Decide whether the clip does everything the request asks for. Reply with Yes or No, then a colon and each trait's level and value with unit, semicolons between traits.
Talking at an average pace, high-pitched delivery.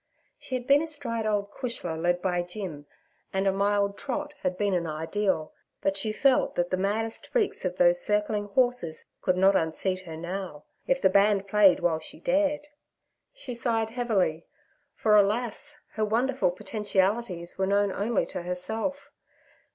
Yes: average, 160 wpm; high, 205 Hz